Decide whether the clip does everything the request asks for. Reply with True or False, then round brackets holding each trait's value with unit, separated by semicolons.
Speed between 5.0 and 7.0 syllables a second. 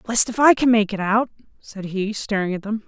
True (5.3 syllables/s)